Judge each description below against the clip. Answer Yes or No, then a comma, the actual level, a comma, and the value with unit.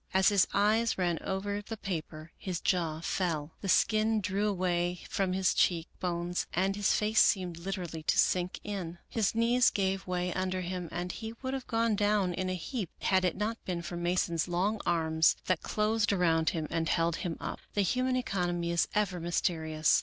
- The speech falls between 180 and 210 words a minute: Yes, average, 190 wpm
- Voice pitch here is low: No, medium, 185 Hz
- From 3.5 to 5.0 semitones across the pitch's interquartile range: No, average, 3.1 semitones